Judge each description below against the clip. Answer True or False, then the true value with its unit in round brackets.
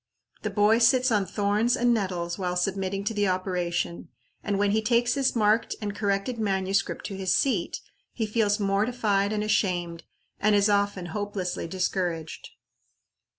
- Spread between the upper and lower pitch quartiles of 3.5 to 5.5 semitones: False (2.4 semitones)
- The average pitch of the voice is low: False (200 Hz)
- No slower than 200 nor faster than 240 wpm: False (150 wpm)